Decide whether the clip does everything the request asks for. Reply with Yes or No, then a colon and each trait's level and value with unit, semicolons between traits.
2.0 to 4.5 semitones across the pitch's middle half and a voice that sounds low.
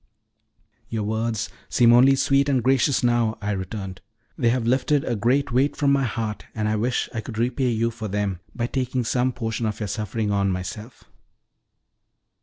Yes: average, 3.0 semitones; low, 115 Hz